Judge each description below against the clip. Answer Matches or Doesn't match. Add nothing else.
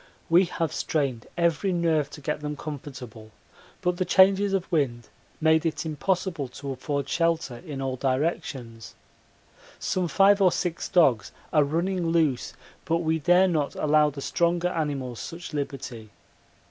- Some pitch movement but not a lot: Matches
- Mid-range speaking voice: Matches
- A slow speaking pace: Doesn't match